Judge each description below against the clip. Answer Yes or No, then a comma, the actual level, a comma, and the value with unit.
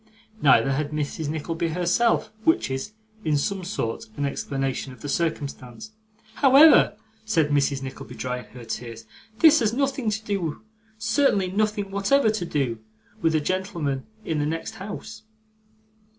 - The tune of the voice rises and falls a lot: Yes, wide, 7.4 semitones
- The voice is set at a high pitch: No, medium, 165 Hz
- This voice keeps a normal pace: Yes, average, 145 wpm